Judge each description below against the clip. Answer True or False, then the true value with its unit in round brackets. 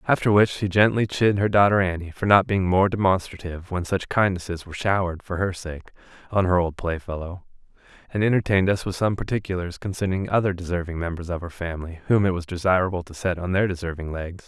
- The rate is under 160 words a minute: False (200 wpm)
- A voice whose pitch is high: False (90 Hz)